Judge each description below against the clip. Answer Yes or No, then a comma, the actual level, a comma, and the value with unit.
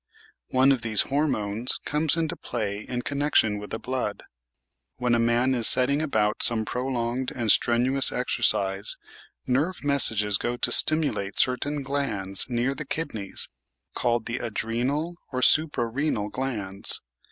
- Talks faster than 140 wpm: No, slow, 135 wpm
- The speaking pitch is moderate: No, low, 125 Hz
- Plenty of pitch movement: No, average, 4.0 semitones